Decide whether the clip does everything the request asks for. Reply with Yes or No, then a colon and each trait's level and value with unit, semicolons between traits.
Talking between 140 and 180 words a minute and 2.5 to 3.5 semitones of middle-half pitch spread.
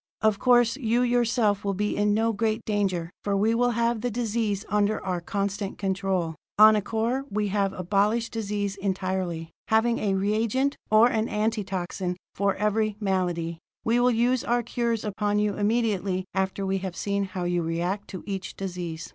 Yes: average, 170 wpm; average, 2.8 semitones